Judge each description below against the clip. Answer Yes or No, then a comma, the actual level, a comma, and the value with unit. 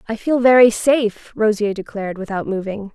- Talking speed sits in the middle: Yes, average, 165 wpm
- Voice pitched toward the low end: No, high, 215 Hz